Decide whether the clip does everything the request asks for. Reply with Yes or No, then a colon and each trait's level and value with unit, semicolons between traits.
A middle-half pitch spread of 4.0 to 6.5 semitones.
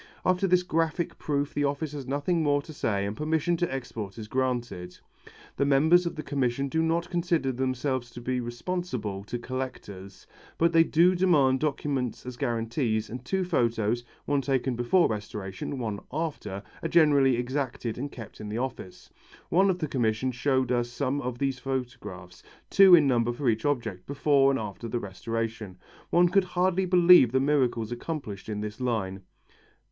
Yes: average, 4.8 semitones